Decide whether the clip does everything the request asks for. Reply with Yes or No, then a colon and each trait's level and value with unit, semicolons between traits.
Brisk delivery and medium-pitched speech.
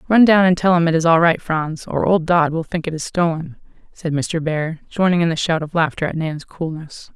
Yes: fast, 250 wpm; medium, 165 Hz